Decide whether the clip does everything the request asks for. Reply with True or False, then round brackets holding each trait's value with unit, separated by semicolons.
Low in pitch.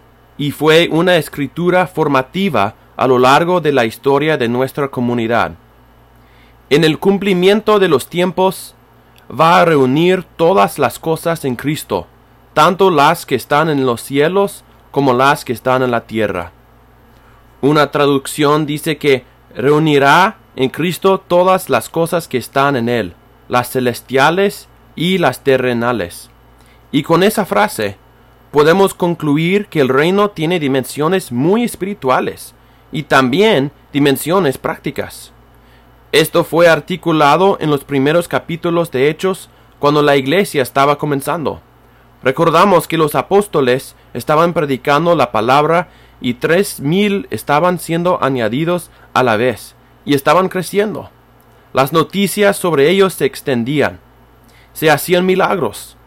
False (145 Hz)